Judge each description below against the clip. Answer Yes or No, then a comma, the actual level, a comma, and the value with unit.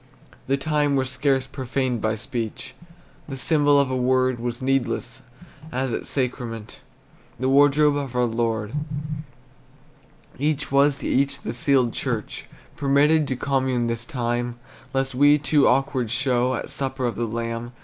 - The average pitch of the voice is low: Yes, low, 130 Hz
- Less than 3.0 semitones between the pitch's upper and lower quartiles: Yes, narrow, 2.6 semitones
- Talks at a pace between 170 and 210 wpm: No, average, 150 wpm